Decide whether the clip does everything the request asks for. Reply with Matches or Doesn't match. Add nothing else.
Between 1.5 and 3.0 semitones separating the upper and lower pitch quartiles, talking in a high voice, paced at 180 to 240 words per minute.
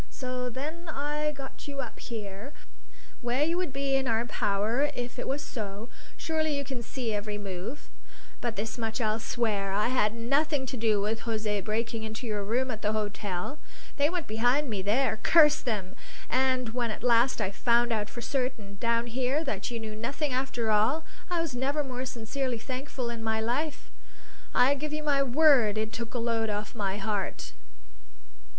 Doesn't match